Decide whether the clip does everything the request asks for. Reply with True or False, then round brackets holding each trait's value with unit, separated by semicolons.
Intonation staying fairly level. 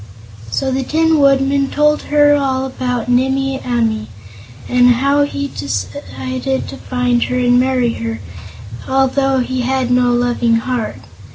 True (1.9 semitones)